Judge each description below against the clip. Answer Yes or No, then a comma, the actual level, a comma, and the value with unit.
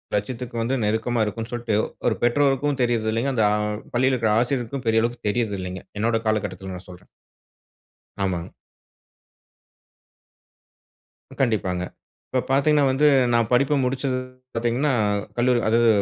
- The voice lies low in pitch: Yes, low, 120 Hz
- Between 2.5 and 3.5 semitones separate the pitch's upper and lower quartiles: Yes, average, 2.8 semitones